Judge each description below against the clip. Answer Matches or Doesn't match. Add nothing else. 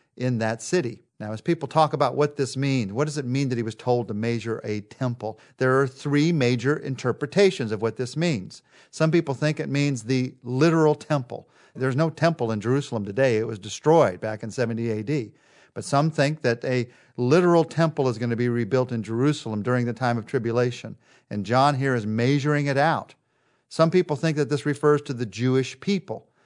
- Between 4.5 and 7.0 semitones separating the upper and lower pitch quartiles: Doesn't match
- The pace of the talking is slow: Doesn't match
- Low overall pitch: Matches